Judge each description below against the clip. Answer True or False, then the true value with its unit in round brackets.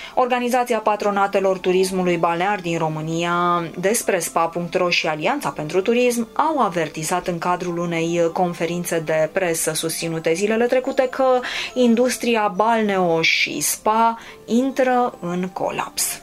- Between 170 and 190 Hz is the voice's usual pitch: True (185 Hz)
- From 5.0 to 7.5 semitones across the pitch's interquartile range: True (5.3 semitones)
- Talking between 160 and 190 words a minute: False (115 wpm)